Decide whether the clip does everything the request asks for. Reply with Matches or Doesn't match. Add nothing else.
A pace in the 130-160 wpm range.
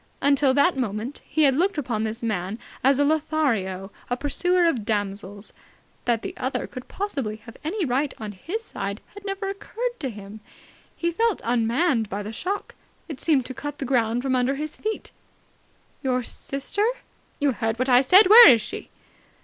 Doesn't match